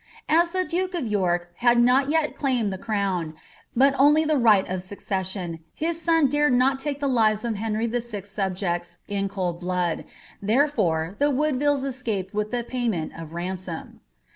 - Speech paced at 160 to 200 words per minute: Yes, average, 165 wpm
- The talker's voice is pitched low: No, high, 220 Hz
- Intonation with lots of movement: Yes, wide, 6.7 semitones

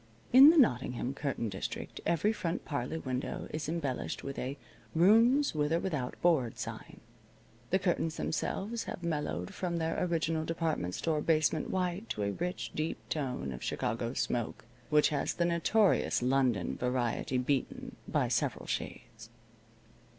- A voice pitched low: No, medium, 155 Hz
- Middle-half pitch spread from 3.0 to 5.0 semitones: No, wide, 5.4 semitones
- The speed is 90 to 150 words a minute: Yes, average, 145 wpm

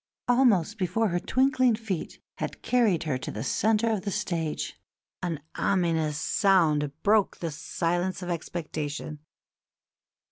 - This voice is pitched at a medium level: Yes, medium, 180 Hz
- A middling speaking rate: No, slow, 130 wpm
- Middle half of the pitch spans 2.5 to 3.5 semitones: No, average, 5.1 semitones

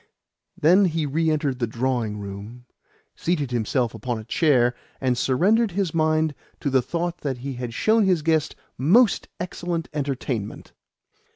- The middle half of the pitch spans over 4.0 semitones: Yes, wide, 5.4 semitones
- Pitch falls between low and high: Yes, medium, 145 Hz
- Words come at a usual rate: Yes, average, 150 wpm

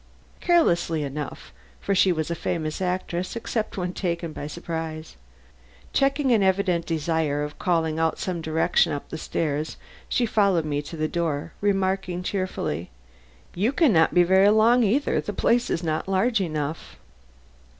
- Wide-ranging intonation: No, average, 3.9 semitones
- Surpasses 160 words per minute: No, average, 150 wpm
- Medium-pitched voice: Yes, medium, 175 Hz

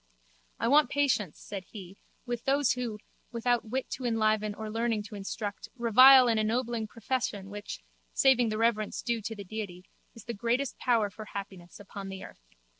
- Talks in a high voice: Yes, high, 225 Hz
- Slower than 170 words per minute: No, average, 175 wpm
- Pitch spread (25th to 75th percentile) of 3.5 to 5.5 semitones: No, average, 2.9 semitones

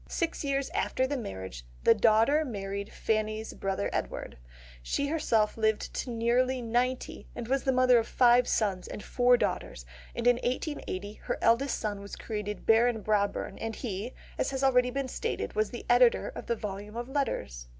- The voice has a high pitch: Yes, high, 235 Hz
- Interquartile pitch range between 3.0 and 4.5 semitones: Yes, average, 3.4 semitones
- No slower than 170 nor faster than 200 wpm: Yes, average, 175 wpm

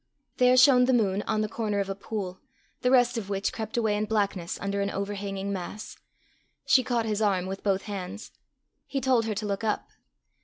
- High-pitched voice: Yes, high, 210 Hz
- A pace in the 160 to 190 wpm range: No, average, 200 wpm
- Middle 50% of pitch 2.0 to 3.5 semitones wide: Yes, narrow, 2.6 semitones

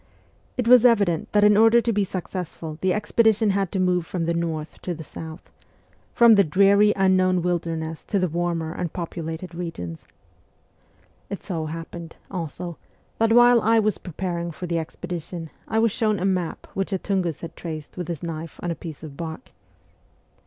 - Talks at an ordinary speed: Yes, average, 180 wpm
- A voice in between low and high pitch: Yes, medium, 180 Hz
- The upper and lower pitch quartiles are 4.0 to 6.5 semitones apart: No, average, 3.4 semitones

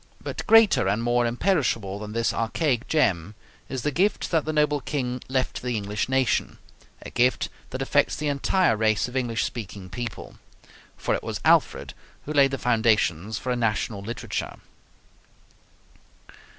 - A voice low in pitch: Yes, low, 120 Hz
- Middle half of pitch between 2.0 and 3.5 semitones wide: No, average, 4.2 semitones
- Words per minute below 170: Yes, average, 160 wpm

